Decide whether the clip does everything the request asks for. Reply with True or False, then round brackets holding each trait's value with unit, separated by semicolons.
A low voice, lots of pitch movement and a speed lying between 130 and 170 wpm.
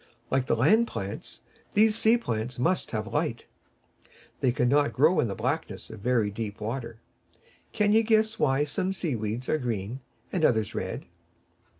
True (125 Hz; 7.7 semitones; 165 wpm)